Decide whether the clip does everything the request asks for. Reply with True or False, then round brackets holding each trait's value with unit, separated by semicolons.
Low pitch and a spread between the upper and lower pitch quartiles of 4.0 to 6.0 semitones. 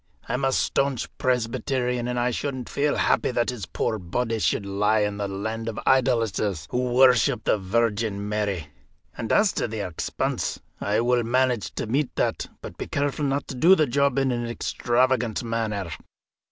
False (120 Hz; 3.3 semitones)